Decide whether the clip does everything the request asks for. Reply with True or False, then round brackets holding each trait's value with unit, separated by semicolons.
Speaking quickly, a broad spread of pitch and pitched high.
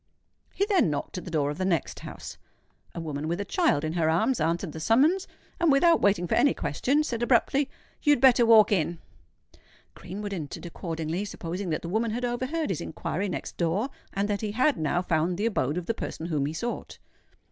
True (210 wpm; 6.7 semitones; 195 Hz)